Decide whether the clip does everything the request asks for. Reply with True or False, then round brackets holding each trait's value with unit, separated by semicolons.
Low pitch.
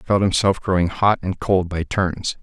True (95 Hz)